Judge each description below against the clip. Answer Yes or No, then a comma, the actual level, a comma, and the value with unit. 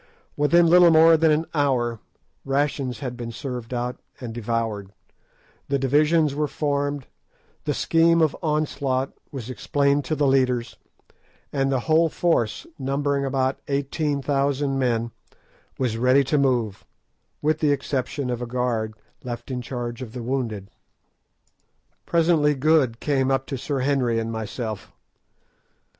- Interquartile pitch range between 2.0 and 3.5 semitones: Yes, average, 3.1 semitones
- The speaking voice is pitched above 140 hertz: No, low, 135 Hz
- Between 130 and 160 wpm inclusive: Yes, slow, 135 wpm